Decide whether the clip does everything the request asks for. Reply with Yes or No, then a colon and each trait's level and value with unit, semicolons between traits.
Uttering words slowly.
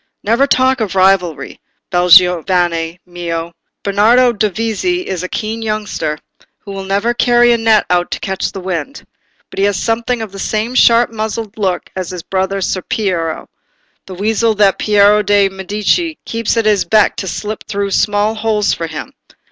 No: average, 170 wpm